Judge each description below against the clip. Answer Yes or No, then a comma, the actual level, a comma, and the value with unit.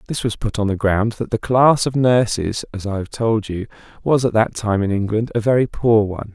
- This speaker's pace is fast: Yes, fast, 245 wpm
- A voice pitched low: Yes, low, 110 Hz